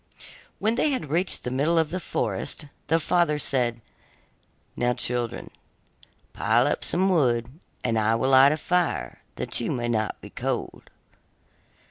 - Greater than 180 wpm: No, average, 150 wpm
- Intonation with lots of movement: Yes, wide, 5.9 semitones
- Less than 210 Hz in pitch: Yes, low, 135 Hz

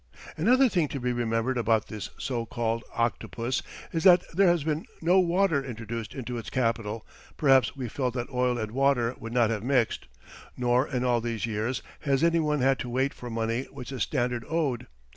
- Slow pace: No, average, 195 wpm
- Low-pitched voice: Yes, low, 125 Hz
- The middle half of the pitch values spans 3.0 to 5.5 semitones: Yes, average, 3.3 semitones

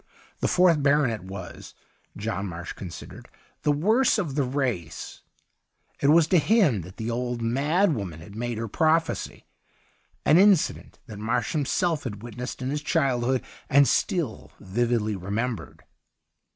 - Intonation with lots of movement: Yes, wide, 6.0 semitones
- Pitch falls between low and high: No, low, 125 Hz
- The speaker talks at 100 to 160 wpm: Yes, average, 145 wpm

